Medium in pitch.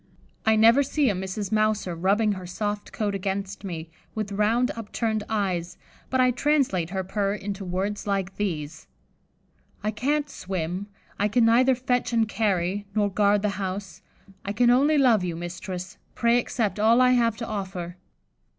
No: high, 205 Hz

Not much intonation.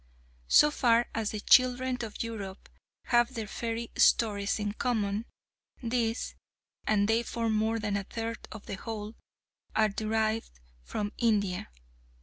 Yes: narrow, 1.9 semitones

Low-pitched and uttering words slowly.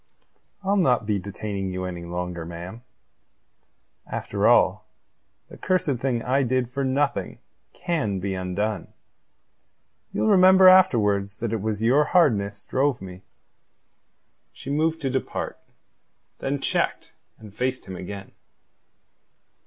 Yes: low, 115 Hz; slow, 120 wpm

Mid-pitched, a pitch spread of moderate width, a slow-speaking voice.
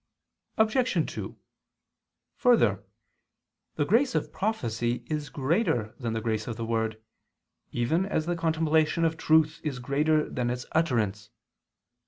No: medium, 150 Hz; wide, 6.0 semitones; slow, 130 wpm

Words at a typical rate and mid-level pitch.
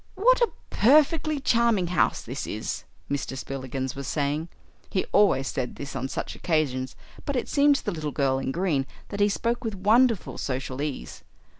Yes: average, 175 wpm; medium, 165 Hz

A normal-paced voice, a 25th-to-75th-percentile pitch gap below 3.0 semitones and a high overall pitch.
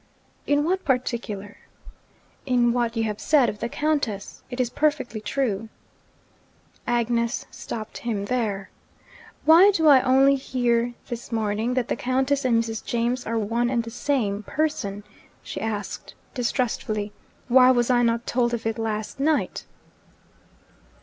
Yes: average, 145 wpm; narrow, 2.6 semitones; high, 240 Hz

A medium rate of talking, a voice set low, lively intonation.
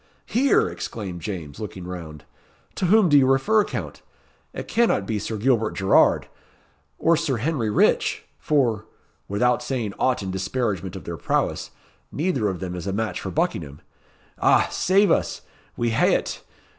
Yes: average, 155 wpm; low, 110 Hz; wide, 6.3 semitones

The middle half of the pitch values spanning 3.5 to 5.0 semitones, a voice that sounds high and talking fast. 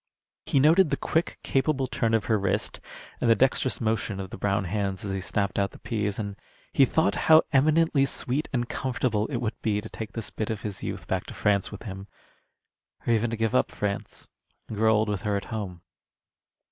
No: average, 4.1 semitones; low, 110 Hz; fast, 210 wpm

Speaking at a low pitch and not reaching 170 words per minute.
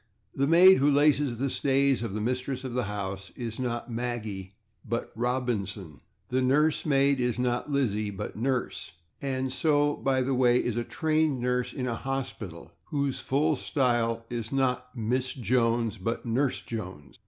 Yes: low, 125 Hz; average, 160 wpm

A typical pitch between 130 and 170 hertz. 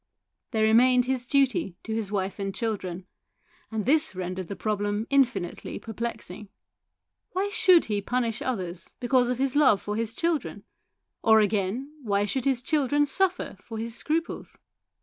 No: high, 230 Hz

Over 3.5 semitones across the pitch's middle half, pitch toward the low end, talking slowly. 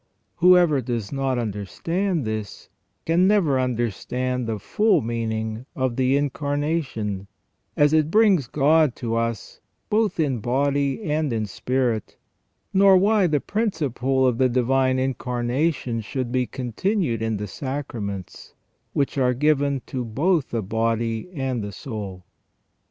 Yes: average, 4.8 semitones; low, 130 Hz; slow, 130 wpm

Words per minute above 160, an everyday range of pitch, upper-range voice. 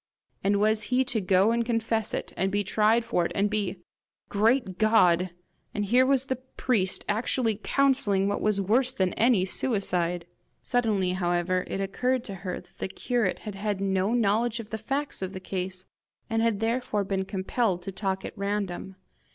Yes: average, 180 wpm; average, 3.4 semitones; high, 205 Hz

